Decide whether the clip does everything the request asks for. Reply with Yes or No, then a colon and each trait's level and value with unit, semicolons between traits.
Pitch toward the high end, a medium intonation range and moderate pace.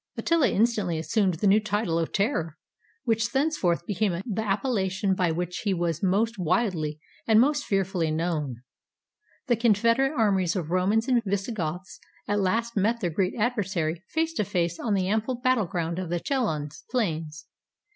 Yes: high, 195 Hz; average, 4.9 semitones; average, 160 wpm